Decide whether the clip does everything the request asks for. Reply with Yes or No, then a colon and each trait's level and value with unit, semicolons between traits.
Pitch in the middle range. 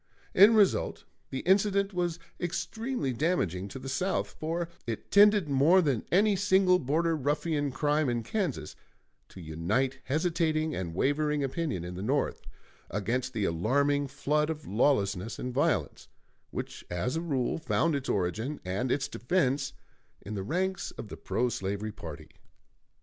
Yes: medium, 145 Hz